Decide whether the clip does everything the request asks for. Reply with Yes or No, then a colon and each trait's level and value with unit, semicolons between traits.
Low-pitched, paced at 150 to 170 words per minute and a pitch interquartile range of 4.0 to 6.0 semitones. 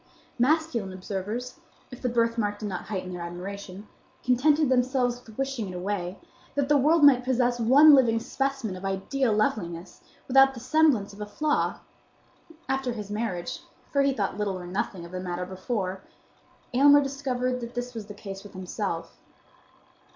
No: high, 230 Hz; average, 160 wpm; average, 5.3 semitones